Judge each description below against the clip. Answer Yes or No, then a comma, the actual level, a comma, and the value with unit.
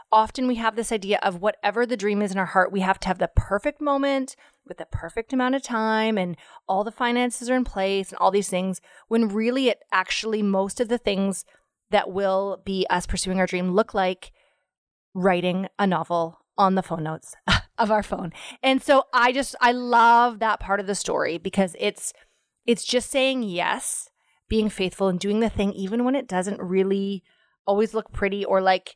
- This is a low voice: No, high, 205 Hz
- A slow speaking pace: No, average, 200 wpm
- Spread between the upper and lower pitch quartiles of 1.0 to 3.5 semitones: No, average, 4.1 semitones